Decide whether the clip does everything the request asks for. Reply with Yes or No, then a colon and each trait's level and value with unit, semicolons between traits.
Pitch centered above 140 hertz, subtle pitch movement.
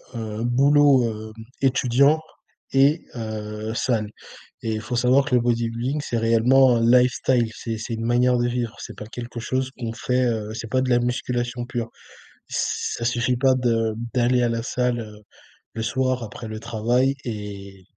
No: low, 120 Hz; narrow, 2.0 semitones